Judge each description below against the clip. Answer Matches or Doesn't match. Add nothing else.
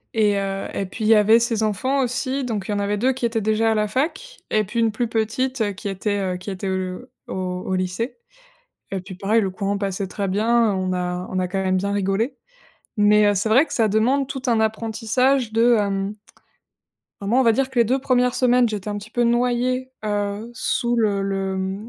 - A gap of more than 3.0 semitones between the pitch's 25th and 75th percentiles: Matches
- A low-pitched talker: Doesn't match